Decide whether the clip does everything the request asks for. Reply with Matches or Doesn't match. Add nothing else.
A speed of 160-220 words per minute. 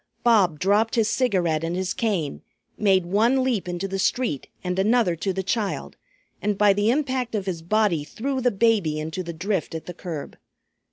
Matches